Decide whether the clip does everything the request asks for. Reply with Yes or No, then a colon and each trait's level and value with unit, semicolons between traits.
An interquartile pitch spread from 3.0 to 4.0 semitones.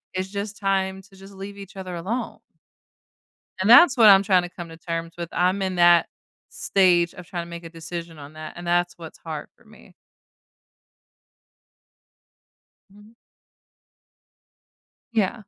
No: narrow, 2.6 semitones